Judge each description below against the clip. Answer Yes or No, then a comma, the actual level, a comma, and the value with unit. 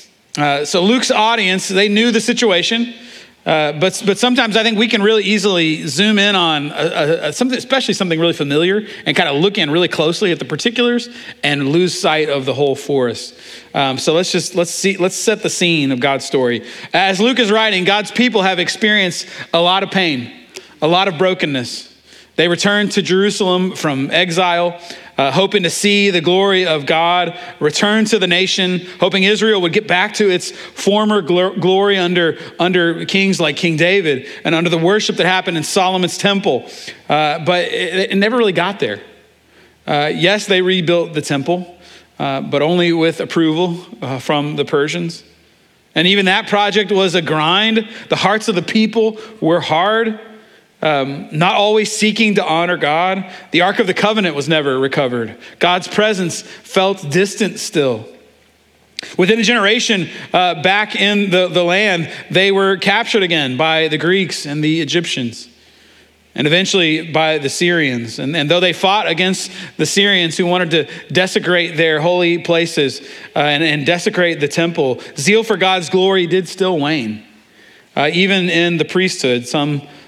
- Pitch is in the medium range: Yes, medium, 180 Hz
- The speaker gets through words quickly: No, average, 175 wpm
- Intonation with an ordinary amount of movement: Yes, average, 4.1 semitones